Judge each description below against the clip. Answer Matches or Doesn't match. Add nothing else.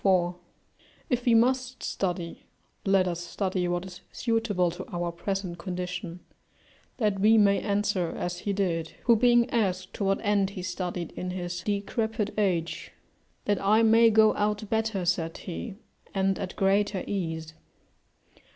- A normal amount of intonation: Matches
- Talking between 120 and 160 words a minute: Matches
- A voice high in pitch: Matches